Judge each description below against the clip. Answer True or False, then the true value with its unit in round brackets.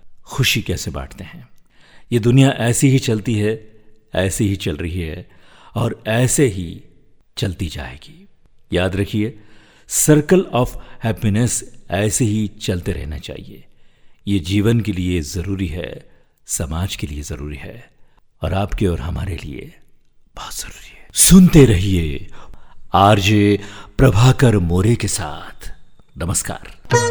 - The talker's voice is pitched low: True (105 Hz)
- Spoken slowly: False (125 wpm)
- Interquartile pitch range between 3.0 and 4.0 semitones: False (4.7 semitones)